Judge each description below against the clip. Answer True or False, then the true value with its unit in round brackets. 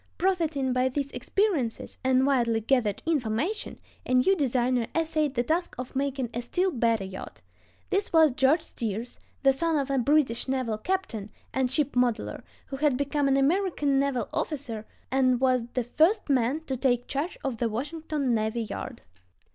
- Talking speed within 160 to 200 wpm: True (165 wpm)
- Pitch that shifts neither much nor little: True (4.0 semitones)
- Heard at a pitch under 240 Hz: False (265 Hz)